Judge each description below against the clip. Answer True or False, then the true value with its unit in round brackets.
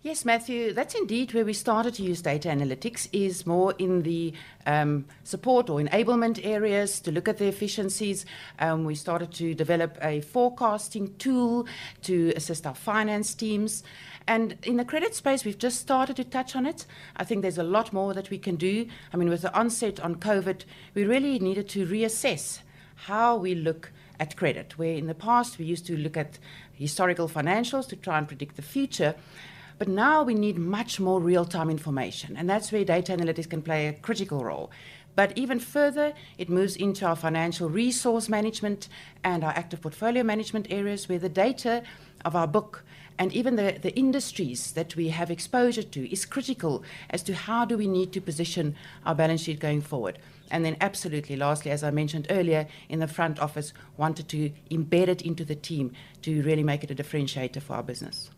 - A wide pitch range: True (5.7 semitones)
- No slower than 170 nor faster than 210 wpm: True (190 wpm)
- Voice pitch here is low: False (180 Hz)